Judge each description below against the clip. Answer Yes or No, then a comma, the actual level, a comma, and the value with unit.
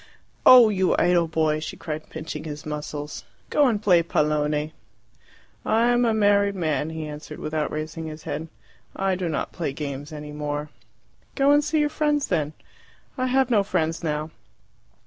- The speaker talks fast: No, average, 165 wpm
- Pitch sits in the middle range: Yes, medium, 160 Hz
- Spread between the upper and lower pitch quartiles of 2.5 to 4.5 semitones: No, wide, 5.5 semitones